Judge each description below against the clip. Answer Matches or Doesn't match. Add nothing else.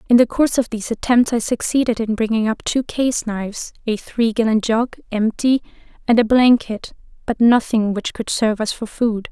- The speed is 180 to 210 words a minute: Matches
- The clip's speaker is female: Matches